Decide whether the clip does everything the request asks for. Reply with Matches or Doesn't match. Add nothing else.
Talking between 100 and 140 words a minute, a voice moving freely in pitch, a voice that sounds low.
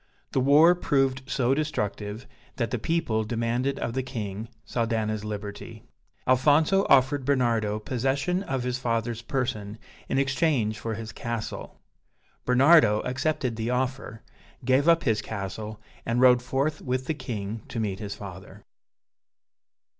Doesn't match